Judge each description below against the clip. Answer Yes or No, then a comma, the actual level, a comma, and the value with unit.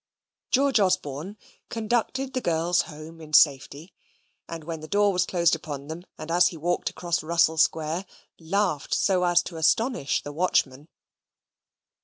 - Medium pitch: Yes, medium, 170 Hz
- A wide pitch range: No, average, 3.3 semitones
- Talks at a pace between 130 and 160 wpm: Yes, average, 150 wpm